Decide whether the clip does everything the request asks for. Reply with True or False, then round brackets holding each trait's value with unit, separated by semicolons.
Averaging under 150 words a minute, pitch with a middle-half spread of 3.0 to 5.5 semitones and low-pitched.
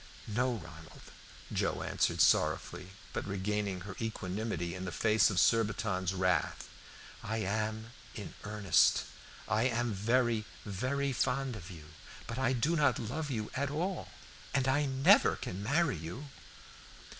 True (140 wpm; 5.2 semitones; 110 Hz)